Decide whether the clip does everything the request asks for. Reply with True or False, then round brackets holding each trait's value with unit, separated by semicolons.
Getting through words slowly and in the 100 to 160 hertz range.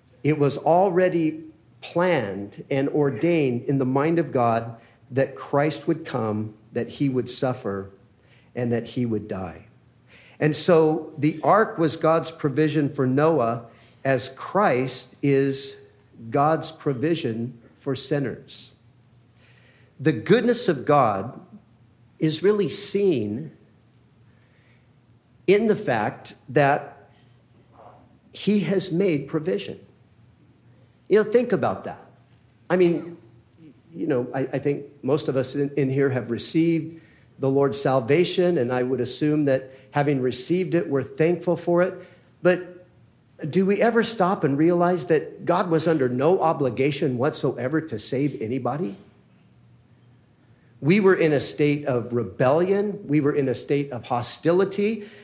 True (130 wpm; 140 Hz)